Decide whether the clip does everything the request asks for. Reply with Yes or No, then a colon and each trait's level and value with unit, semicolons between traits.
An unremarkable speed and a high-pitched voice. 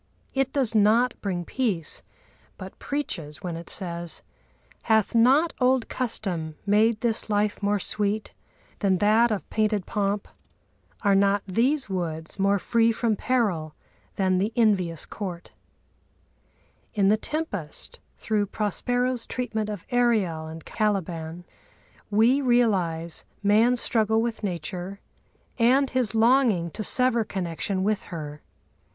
No: slow, 125 wpm; high, 210 Hz